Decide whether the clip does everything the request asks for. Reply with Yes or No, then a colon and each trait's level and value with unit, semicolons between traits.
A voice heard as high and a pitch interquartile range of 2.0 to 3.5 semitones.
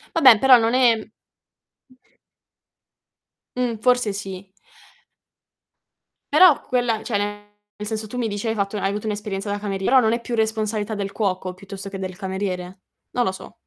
Yes: high, 210 Hz; narrow, 2.6 semitones